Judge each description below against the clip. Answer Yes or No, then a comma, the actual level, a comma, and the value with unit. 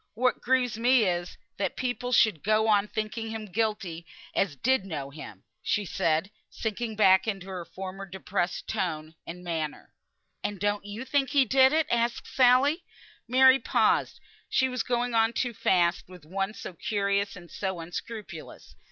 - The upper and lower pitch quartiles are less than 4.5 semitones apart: No, average, 5.1 semitones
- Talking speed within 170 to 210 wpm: No, average, 160 wpm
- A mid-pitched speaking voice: No, high, 210 Hz